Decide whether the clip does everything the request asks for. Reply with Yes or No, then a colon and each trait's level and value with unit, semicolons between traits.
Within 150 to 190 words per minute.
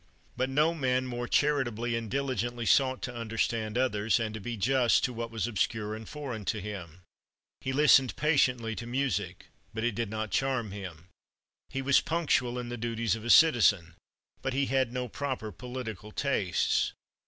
Yes: average, 175 wpm